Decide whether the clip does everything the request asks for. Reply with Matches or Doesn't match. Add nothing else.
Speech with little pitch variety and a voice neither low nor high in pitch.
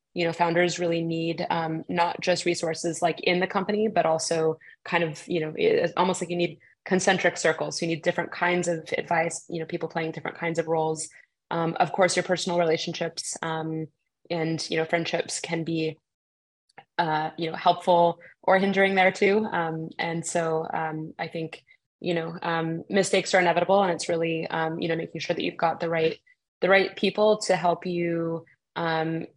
Matches